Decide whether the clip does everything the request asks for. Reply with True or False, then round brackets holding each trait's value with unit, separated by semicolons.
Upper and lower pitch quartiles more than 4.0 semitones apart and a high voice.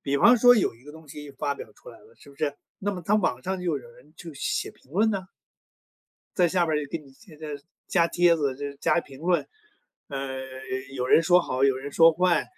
False (4.6 semitones; 155 Hz)